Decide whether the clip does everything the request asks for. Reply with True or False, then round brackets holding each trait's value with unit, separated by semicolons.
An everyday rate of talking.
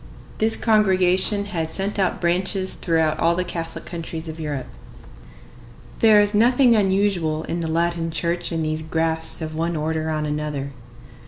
True (155 wpm)